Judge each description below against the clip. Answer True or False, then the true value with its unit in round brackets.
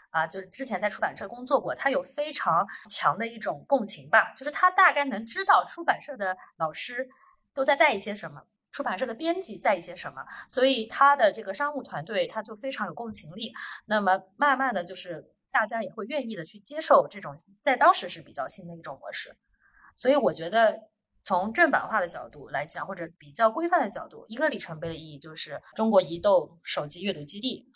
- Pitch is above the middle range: True (225 Hz)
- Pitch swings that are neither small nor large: False (7.3 semitones)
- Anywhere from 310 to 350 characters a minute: True (320 characters per minute)